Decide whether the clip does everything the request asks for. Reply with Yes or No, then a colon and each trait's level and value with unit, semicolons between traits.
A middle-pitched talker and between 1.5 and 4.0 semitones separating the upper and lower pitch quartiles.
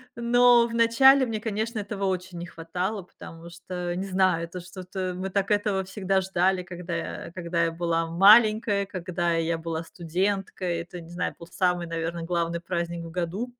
Yes: medium, 180 Hz; average, 2.8 semitones